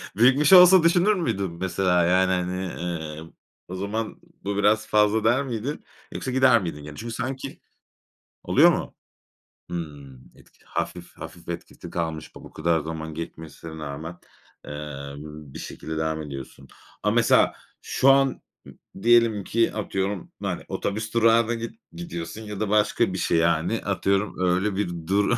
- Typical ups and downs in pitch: No, wide, 5.9 semitones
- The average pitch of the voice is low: Yes, very low, 95 Hz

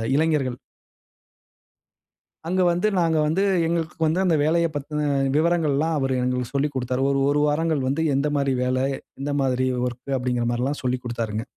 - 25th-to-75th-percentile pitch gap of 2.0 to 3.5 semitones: No, average, 4.1 semitones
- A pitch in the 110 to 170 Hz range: Yes, medium, 140 Hz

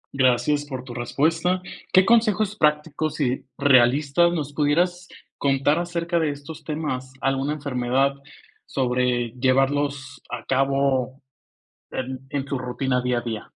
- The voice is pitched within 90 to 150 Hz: Yes, medium, 140 Hz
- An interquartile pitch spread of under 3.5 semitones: Yes, average, 3.1 semitones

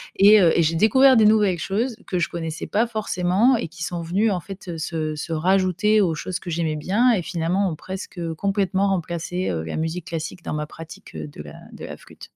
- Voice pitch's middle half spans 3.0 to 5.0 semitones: Yes, average, 3.6 semitones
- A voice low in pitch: No, medium, 180 Hz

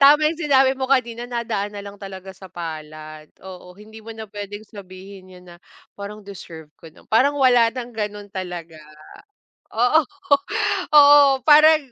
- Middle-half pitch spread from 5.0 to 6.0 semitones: Yes, wide, 5.4 semitones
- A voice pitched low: No, high, 205 Hz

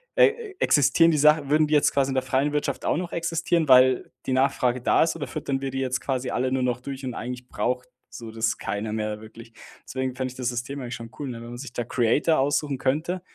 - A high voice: No, low, 130 Hz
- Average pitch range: Yes, average, 3.2 semitones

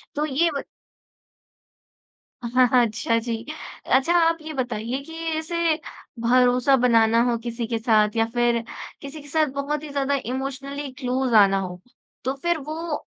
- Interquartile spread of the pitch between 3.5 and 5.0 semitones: Yes, average, 3.9 semitones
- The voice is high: Yes, very high, 260 Hz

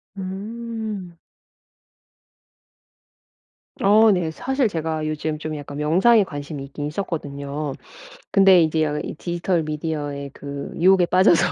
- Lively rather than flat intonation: No, average, 4.4 semitones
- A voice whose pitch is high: No, medium, 165 Hz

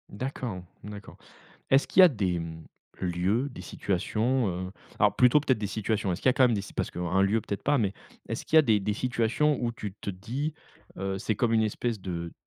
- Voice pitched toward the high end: No, low, 105 Hz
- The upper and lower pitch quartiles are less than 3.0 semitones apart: No, average, 4.7 semitones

